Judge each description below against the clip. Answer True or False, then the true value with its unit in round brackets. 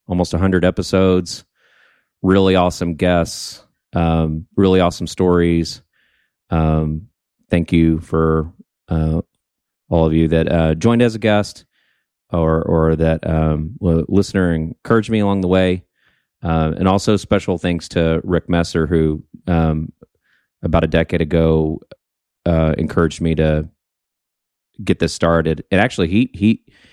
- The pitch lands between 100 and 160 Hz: False (85 Hz)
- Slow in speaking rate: True (130 wpm)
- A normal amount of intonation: False (2.3 semitones)